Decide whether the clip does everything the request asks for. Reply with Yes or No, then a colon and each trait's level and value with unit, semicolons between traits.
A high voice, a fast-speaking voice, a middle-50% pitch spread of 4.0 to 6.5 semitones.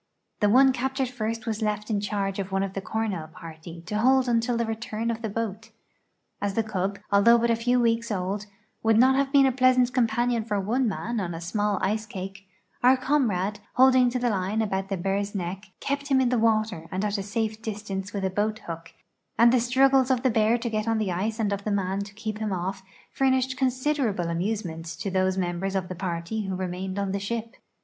No: high, 215 Hz; fast, 225 wpm; average, 3.6 semitones